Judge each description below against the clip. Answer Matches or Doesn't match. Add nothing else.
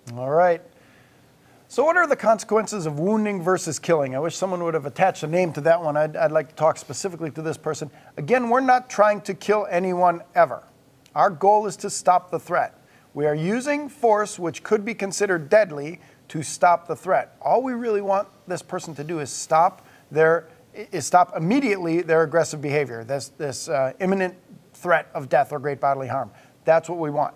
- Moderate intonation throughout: Matches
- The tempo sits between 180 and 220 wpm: Matches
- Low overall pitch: Doesn't match